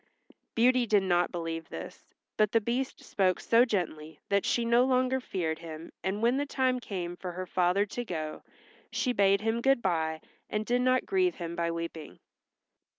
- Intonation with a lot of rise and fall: Yes, wide, 6.2 semitones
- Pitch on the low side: No, high, 200 Hz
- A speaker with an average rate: Yes, average, 180 wpm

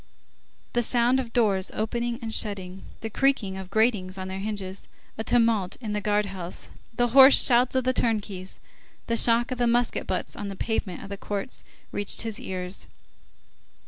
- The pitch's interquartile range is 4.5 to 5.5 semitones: No, average, 3.7 semitones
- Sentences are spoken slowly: No, average, 175 wpm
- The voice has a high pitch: Yes, high, 220 Hz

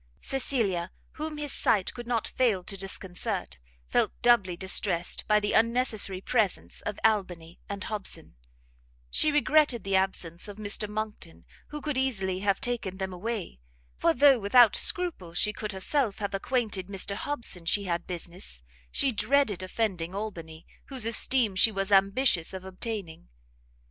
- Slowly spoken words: No, average, 150 wpm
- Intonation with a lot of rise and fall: No, average, 4.1 semitones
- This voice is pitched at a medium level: No, high, 205 Hz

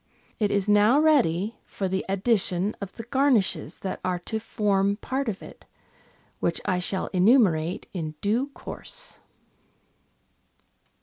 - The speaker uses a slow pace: Yes, slow, 130 wpm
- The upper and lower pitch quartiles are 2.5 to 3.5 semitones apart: No, average, 3.9 semitones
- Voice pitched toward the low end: No, high, 200 Hz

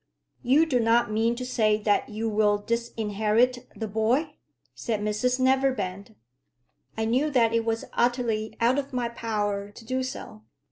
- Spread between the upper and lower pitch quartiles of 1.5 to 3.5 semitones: Yes, average, 2.8 semitones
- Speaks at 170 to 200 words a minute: No, average, 155 wpm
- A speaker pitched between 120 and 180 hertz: No, high, 230 Hz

